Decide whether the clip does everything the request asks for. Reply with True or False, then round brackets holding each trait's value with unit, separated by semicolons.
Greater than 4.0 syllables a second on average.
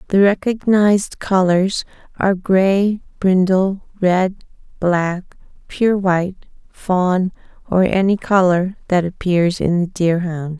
False (3.6 syllables/s)